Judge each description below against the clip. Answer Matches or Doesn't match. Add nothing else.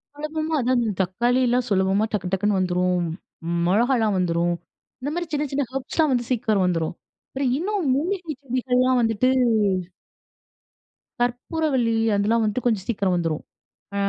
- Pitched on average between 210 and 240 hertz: Matches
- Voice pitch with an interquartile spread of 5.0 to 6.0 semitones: Matches